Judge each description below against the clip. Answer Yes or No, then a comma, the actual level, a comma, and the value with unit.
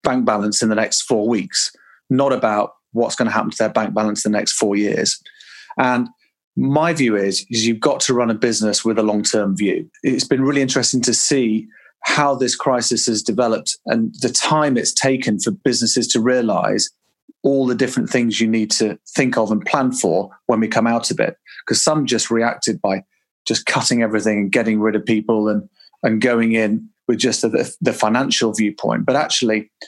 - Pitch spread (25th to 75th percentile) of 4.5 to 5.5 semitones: No, average, 2.7 semitones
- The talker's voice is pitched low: Yes, low, 115 Hz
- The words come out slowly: No, fast, 205 wpm